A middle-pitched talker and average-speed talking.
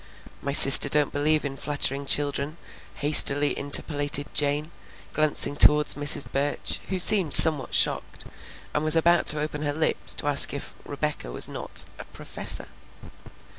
Yes: medium, 145 Hz; average, 145 wpm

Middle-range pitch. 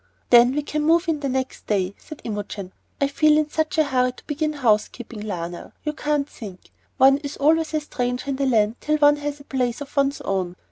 No: very high, 275 Hz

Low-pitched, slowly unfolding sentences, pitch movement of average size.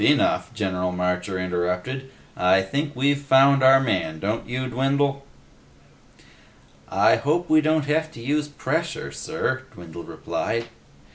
No: low, 130 Hz; slow, 130 wpm; wide, 7.6 semitones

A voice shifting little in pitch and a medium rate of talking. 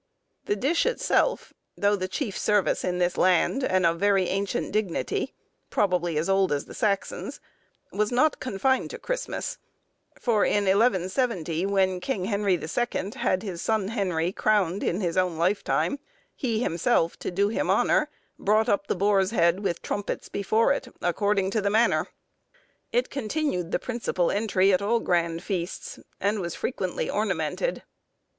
No: average, 3.3 semitones; average, 155 wpm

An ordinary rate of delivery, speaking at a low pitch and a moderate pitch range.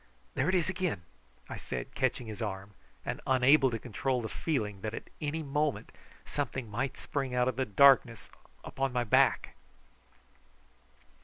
Yes: average, 155 wpm; low, 130 Hz; average, 4.0 semitones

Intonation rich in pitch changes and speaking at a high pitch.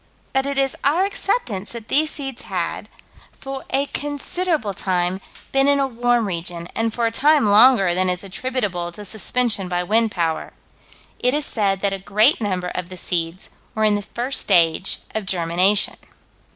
Yes: wide, 6.4 semitones; high, 215 Hz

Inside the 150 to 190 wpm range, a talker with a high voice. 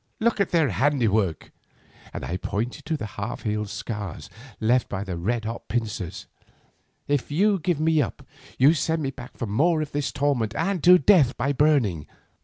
No: average, 180 wpm; low, 125 Hz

